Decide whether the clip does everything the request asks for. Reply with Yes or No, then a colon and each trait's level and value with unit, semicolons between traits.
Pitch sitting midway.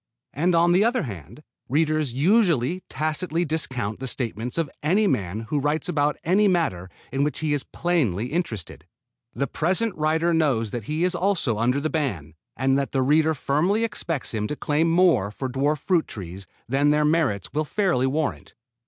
Yes: medium, 150 Hz